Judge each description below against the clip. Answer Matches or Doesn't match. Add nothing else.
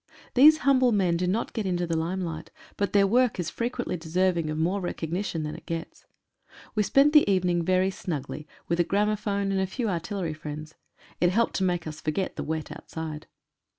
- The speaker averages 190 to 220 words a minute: Matches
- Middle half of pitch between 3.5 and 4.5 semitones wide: Matches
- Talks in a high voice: Doesn't match